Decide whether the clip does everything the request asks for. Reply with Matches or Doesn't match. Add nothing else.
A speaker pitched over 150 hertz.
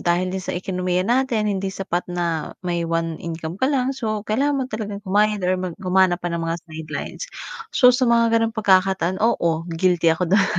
Matches